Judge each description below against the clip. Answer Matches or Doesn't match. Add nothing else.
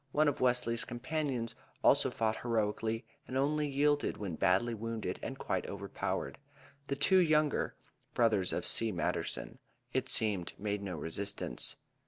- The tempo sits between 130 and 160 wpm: Matches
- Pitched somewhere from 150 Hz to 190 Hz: Doesn't match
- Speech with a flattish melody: Doesn't match